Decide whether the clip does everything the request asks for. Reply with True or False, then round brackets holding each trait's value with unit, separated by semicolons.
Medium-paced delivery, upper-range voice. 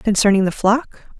True (150 wpm; 215 Hz)